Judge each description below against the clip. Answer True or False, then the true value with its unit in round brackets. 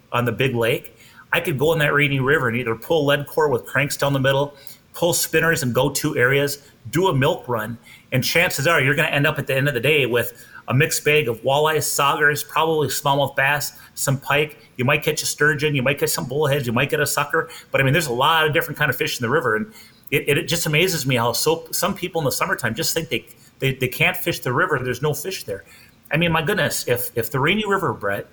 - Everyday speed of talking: False (260 wpm)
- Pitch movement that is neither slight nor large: True (3.8 semitones)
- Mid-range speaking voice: True (145 Hz)